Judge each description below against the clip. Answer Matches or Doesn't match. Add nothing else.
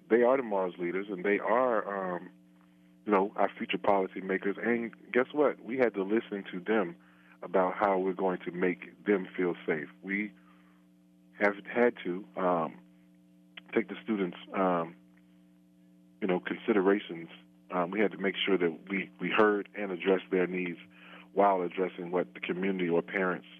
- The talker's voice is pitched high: Doesn't match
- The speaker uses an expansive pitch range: Matches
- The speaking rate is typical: Matches